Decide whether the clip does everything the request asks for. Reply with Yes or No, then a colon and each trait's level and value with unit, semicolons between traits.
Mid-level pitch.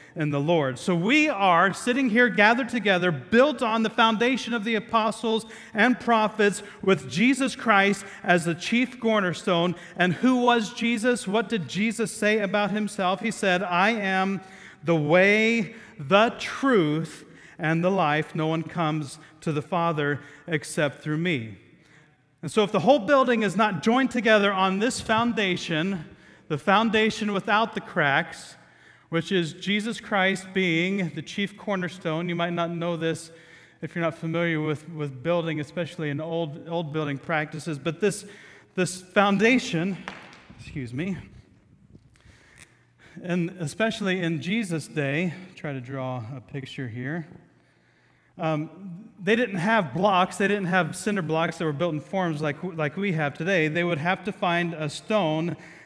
Yes: medium, 180 Hz